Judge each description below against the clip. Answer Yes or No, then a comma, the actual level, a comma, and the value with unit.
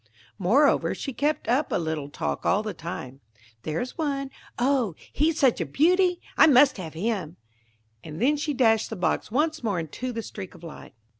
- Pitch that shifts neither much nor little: No, wide, 8.4 semitones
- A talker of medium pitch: No, high, 235 Hz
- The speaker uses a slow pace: No, average, 170 wpm